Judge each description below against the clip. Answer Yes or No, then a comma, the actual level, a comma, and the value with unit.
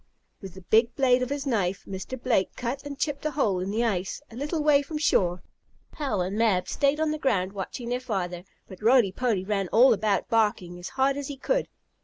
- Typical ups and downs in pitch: No, wide, 6.3 semitones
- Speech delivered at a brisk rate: Yes, fast, 220 wpm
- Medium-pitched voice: No, high, 230 Hz